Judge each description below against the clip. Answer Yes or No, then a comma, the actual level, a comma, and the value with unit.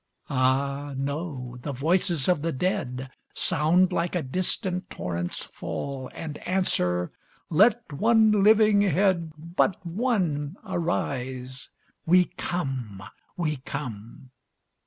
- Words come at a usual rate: No, slow, 105 wpm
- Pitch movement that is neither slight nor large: No, wide, 5.8 semitones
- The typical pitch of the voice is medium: Yes, medium, 155 Hz